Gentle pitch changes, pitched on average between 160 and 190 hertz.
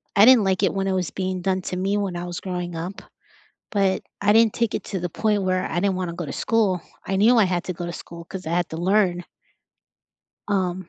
Yes: narrow, 2.2 semitones; medium, 185 Hz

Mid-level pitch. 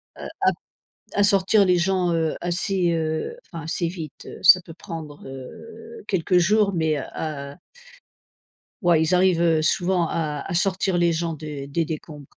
Yes: medium, 170 Hz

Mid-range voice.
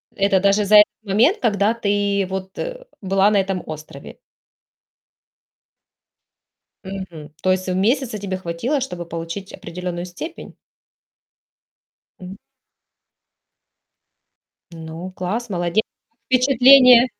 No: high, 195 Hz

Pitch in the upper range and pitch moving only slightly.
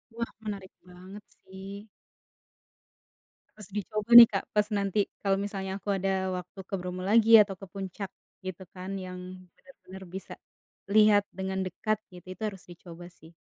Yes: high, 195 Hz; narrow, 2.0 semitones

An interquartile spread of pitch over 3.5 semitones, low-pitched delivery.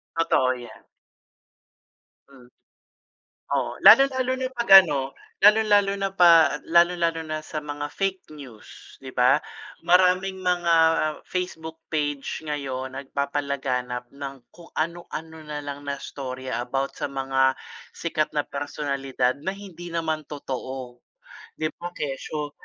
No: average, 4.3 semitones; medium, 150 Hz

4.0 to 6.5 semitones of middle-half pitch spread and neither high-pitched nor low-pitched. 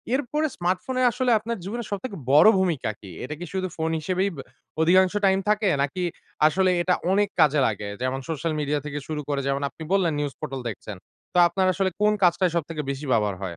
Yes: average, 5.0 semitones; medium, 170 Hz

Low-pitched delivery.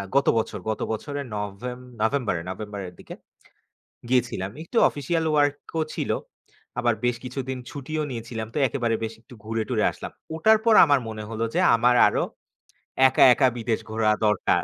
Yes: low, 120 Hz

